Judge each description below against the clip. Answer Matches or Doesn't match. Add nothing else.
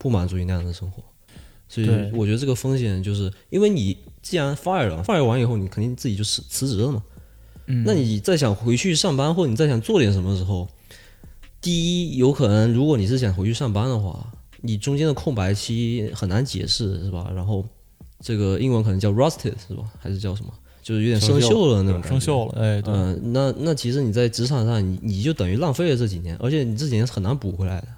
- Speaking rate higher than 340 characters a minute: Matches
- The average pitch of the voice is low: Matches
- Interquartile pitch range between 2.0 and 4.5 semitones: Doesn't match